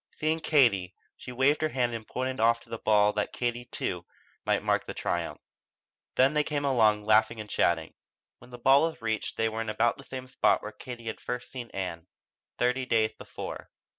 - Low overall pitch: Yes, low, 120 Hz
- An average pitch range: Yes, average, 3.3 semitones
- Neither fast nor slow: Yes, average, 195 wpm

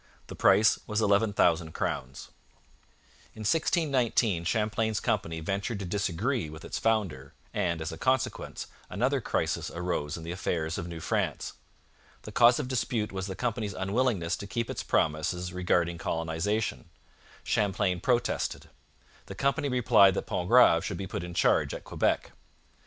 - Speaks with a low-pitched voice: Yes, low, 100 Hz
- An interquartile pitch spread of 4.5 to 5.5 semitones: Yes, average, 5.1 semitones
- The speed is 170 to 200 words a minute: No, average, 145 wpm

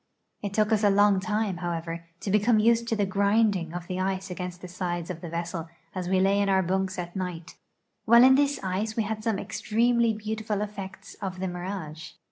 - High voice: Yes, high, 195 Hz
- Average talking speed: No, fast, 210 wpm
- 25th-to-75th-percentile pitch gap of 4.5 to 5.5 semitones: No, average, 3.0 semitones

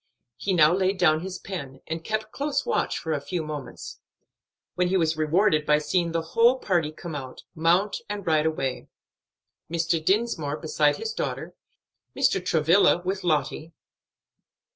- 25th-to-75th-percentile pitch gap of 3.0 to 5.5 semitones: Yes, average, 3.7 semitones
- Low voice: No, medium, 165 Hz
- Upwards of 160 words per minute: No, average, 155 wpm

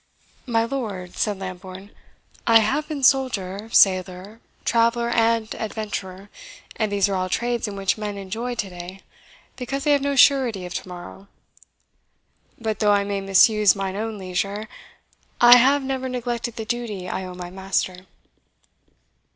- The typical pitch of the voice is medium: No, high, 210 Hz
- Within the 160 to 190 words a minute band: No, average, 150 wpm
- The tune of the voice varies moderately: Yes, average, 3.8 semitones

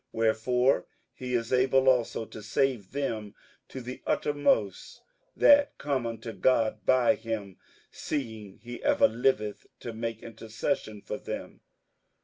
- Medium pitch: No, low, 120 Hz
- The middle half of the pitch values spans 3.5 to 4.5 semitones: No, average, 3.1 semitones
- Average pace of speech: No, slow, 130 wpm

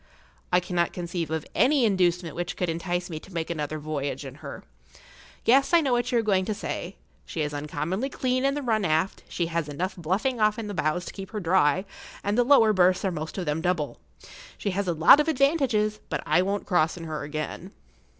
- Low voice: No, medium, 180 Hz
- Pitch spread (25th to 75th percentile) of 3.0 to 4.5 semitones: No, average, 4.9 semitones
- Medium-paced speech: No, fast, 220 wpm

